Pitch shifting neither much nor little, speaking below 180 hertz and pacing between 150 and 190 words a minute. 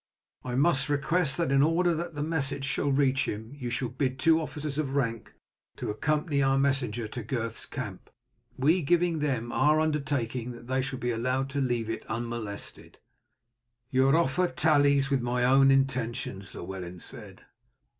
Yes: average, 3.5 semitones; low, 135 Hz; average, 155 wpm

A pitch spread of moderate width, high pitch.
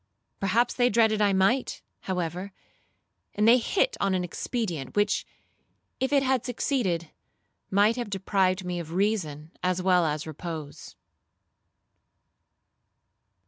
Yes: average, 4.6 semitones; high, 195 Hz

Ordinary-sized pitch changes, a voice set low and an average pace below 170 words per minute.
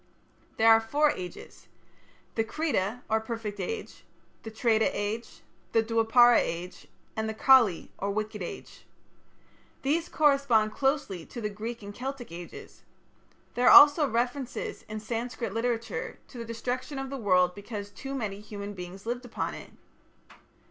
No: average, 3.6 semitones; high, 225 Hz; average, 150 wpm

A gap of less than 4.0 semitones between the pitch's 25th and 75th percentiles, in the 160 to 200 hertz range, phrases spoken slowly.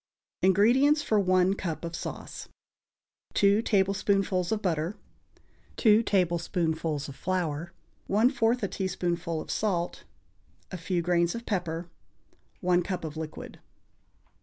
Yes: average, 3.1 semitones; medium, 185 Hz; slow, 115 wpm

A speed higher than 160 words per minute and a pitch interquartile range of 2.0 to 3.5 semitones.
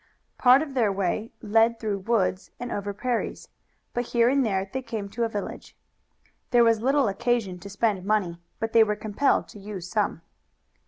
Yes: average, 180 wpm; average, 3.1 semitones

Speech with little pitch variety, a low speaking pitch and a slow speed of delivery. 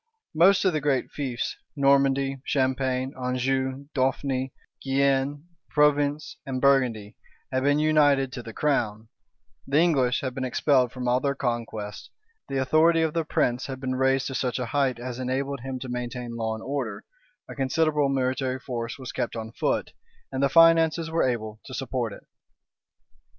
No: narrow, 2.1 semitones; low, 130 Hz; average, 165 wpm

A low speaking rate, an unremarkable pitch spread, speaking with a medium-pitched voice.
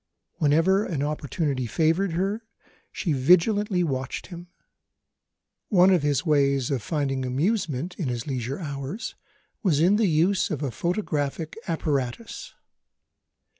Yes: slow, 125 wpm; average, 5.0 semitones; medium, 155 Hz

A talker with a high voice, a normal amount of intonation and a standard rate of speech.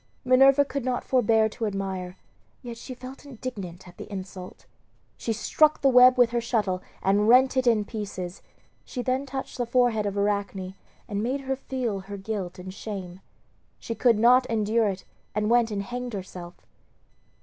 Yes: high, 225 Hz; average, 4.3 semitones; average, 170 wpm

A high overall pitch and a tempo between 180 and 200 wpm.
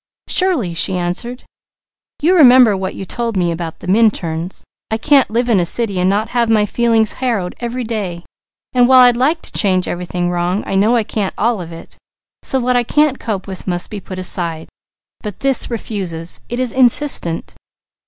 Yes: high, 215 Hz; average, 190 wpm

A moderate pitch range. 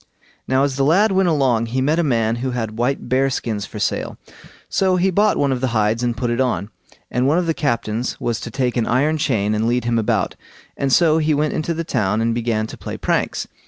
Yes: average, 4.7 semitones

